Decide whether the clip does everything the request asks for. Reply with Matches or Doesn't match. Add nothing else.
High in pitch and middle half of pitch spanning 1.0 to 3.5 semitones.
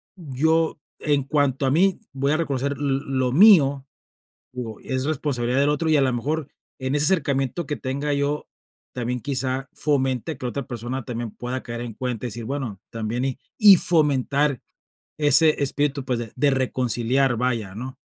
Doesn't match